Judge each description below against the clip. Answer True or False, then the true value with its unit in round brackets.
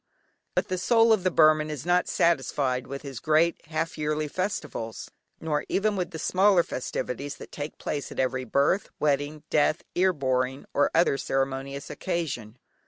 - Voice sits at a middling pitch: True (150 Hz)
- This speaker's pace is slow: False (165 wpm)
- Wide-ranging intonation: False (4.1 semitones)